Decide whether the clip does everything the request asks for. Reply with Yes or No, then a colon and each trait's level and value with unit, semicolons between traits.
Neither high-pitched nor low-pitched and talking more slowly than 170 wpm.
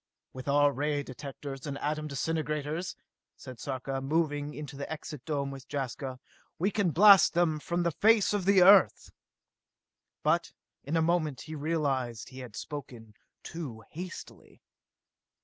Yes: medium, 150 Hz; average, 150 wpm